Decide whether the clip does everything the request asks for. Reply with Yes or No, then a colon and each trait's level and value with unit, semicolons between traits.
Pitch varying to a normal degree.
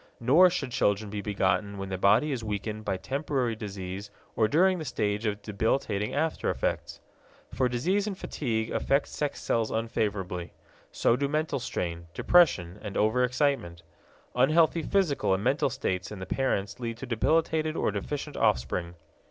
No: wide, 5.8 semitones